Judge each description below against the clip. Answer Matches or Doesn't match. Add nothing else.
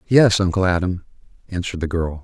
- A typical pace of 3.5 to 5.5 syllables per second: Doesn't match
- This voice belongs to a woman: Doesn't match